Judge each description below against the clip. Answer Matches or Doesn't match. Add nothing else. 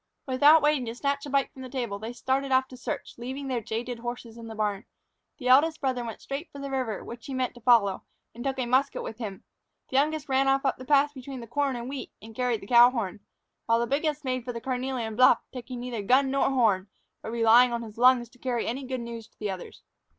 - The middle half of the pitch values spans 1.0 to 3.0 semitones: Matches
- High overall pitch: Matches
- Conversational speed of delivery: Doesn't match